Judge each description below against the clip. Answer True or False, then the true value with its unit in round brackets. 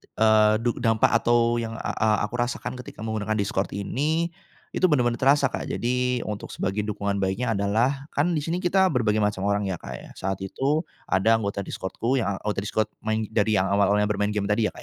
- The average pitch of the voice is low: True (110 Hz)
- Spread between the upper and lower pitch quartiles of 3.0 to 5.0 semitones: True (3.5 semitones)